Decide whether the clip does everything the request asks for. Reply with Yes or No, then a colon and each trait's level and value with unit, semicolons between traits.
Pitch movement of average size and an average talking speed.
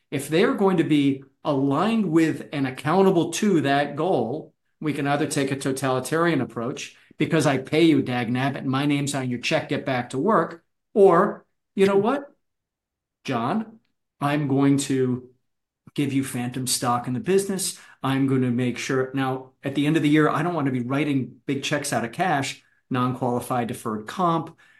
Yes: average, 4.0 semitones; average, 185 wpm